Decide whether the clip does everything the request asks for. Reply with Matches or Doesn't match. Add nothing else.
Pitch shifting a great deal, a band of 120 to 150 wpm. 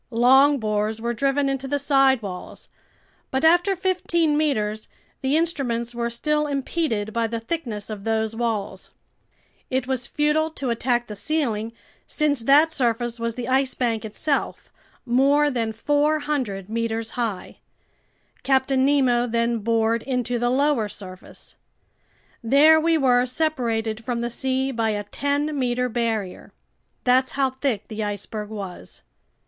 Doesn't match